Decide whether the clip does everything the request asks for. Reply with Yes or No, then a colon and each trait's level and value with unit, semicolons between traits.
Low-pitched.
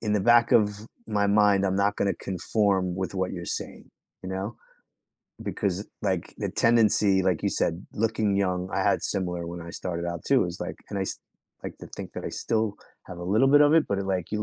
Yes: low, 100 Hz